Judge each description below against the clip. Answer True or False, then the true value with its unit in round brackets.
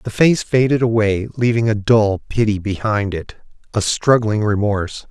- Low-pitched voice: True (110 Hz)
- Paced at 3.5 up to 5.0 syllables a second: True (4.7 syllables/s)